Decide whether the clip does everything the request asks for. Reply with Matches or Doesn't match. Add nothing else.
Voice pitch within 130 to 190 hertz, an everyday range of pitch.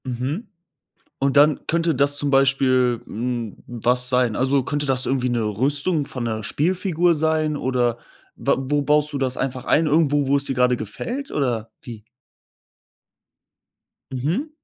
Matches